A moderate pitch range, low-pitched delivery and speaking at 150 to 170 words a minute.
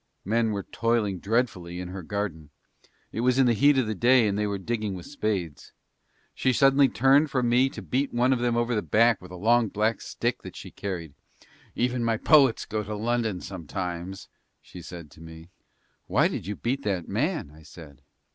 No: average, 4.9 semitones; low, 110 Hz; average, 200 wpm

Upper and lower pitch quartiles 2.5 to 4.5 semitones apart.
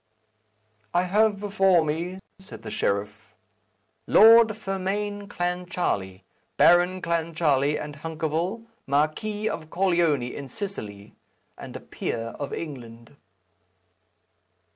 No: average, 5.3 semitones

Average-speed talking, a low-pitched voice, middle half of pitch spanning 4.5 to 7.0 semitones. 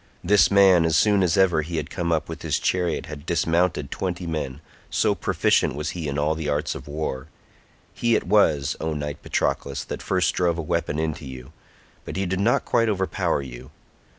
No: average, 195 wpm; very low, 80 Hz; average, 3.7 semitones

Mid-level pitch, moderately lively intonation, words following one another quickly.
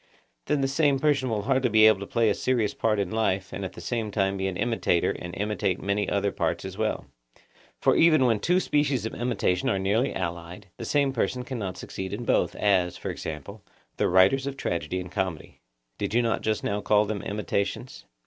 No: low, 105 Hz; average, 4.6 semitones; fast, 210 wpm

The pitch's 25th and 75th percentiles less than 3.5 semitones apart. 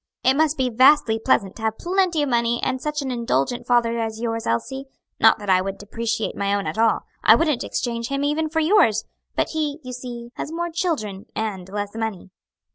No: average, 4.8 semitones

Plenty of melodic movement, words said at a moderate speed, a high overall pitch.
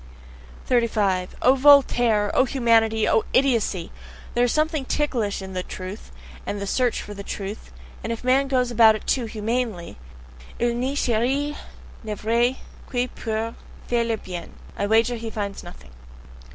No: average, 3.3 semitones; average, 160 wpm; high, 230 Hz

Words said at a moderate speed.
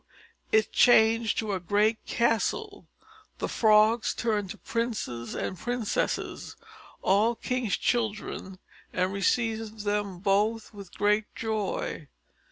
No: slow, 110 wpm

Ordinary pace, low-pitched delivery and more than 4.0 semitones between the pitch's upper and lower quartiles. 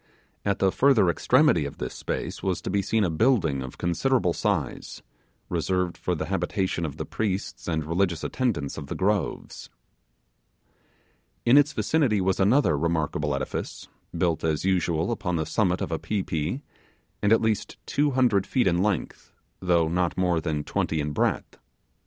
Yes: average, 165 wpm; very low, 90 Hz; average, 4.6 semitones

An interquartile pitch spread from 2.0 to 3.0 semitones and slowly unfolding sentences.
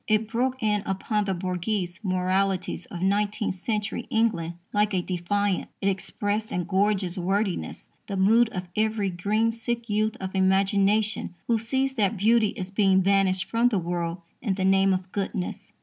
No: narrow, 2.5 semitones; average, 165 wpm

